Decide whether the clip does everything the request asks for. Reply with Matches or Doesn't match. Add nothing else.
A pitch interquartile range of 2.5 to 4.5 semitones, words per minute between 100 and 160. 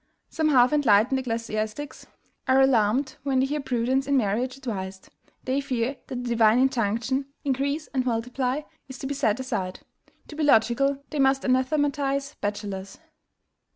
Matches